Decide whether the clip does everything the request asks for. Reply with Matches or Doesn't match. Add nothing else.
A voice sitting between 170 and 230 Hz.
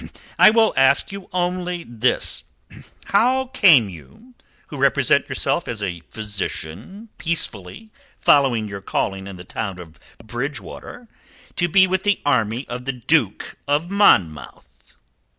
Doesn't match